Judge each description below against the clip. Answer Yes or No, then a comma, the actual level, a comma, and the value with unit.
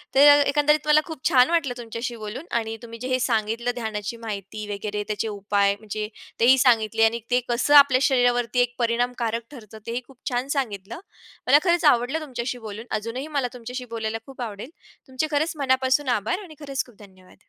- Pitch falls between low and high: No, high, 245 Hz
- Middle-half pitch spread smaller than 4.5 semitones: Yes, average, 3.3 semitones